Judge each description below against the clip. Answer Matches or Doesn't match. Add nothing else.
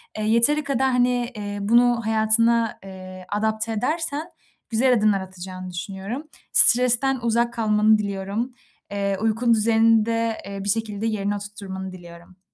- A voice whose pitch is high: Matches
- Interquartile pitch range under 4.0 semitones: Matches